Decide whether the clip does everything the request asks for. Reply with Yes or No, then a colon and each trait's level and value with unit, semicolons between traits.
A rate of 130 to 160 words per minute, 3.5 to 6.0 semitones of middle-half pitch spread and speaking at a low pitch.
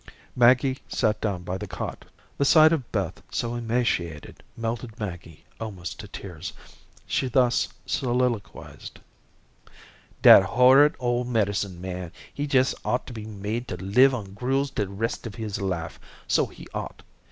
Yes: average, 150 wpm; average, 4.5 semitones; low, 115 Hz